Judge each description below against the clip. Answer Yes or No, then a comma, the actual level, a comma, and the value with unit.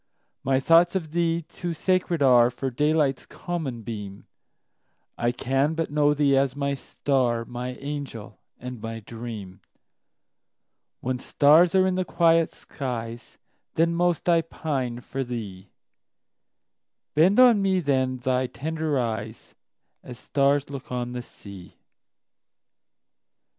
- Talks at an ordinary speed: No, slow, 110 wpm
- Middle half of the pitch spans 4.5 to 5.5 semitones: Yes, average, 5.0 semitones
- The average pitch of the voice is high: No, low, 135 Hz